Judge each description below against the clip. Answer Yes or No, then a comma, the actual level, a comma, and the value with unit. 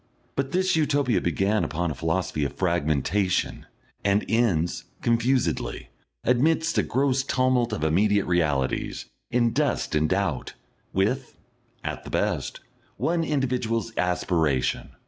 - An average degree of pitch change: No, wide, 7.0 semitones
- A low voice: Yes, low, 105 Hz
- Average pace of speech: No, slow, 120 wpm